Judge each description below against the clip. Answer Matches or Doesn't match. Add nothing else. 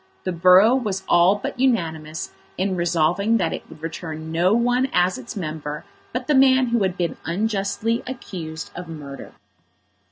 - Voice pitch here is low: Doesn't match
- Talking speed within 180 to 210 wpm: Doesn't match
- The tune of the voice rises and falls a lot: Matches